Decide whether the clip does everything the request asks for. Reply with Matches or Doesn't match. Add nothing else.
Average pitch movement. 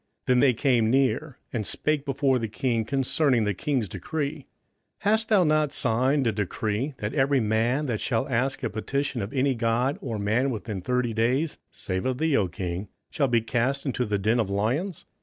Matches